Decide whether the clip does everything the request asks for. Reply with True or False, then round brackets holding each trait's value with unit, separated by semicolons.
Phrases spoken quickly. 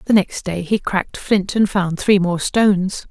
True (210 wpm)